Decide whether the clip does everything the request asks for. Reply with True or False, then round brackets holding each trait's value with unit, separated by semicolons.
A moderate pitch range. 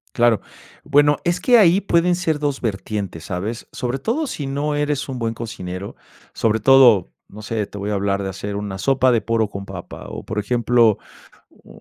False (6.0 semitones)